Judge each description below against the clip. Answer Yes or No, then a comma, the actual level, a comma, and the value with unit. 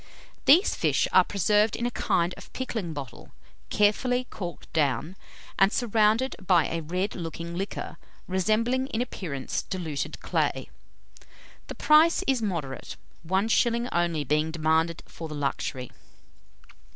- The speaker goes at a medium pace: No, slow, 130 wpm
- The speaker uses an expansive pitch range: Yes, wide, 5.9 semitones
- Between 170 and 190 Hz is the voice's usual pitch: Yes, medium, 185 Hz